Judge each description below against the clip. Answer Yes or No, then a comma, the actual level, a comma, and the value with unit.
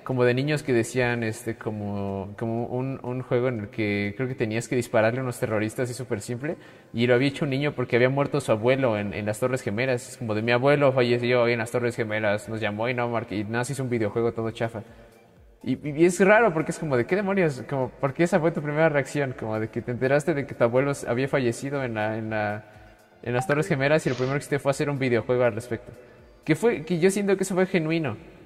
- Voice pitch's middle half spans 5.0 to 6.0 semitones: No, average, 3.7 semitones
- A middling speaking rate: No, fast, 245 wpm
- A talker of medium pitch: No, low, 125 Hz